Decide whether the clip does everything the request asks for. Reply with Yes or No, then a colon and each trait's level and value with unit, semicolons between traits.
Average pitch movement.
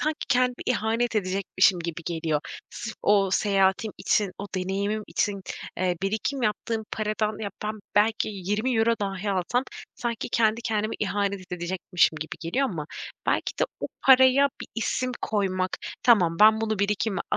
Yes: average, 3.0 semitones